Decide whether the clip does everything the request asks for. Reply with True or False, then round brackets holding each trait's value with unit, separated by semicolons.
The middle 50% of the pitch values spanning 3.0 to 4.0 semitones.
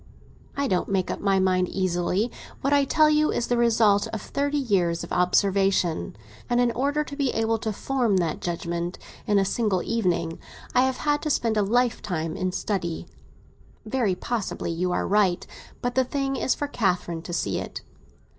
False (5.6 semitones)